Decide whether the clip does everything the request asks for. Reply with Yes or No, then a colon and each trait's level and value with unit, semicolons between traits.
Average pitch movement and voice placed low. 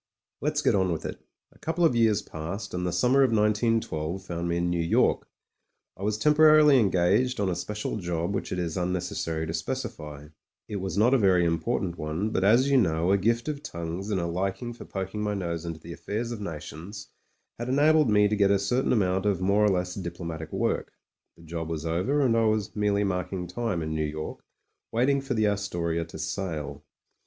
Yes: average, 4.7 semitones; very low, 95 Hz